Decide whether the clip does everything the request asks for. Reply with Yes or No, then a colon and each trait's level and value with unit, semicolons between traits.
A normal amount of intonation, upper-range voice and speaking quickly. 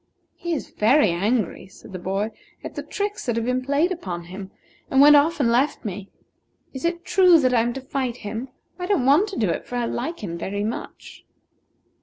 No: wide, 6.6 semitones; very high, 250 Hz; fast, 215 wpm